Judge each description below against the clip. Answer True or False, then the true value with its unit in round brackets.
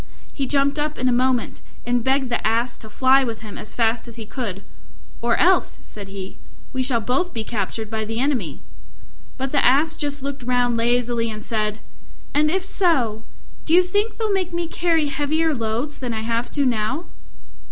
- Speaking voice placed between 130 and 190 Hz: False (250 Hz)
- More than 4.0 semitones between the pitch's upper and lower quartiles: True (4.6 semitones)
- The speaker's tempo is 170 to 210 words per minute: True (195 wpm)